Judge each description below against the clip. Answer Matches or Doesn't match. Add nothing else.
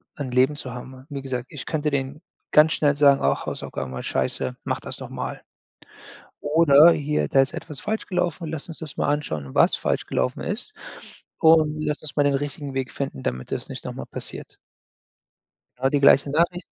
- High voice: Doesn't match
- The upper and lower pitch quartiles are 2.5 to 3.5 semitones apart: Matches